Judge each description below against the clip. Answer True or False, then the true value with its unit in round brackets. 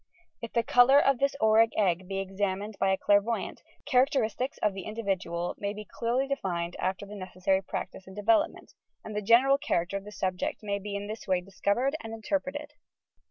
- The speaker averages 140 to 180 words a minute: False (190 wpm)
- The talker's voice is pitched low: False (205 Hz)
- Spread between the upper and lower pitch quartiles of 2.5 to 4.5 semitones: True (3.4 semitones)